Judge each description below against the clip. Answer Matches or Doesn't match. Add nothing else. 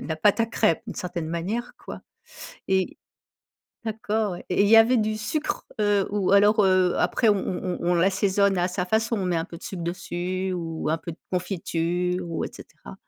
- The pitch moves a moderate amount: Matches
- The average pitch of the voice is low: Doesn't match